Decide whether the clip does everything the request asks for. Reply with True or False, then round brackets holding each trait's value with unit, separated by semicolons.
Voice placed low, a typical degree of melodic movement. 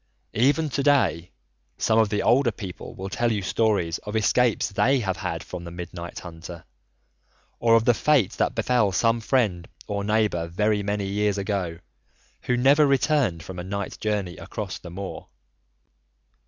True (105 Hz; 4.4 semitones)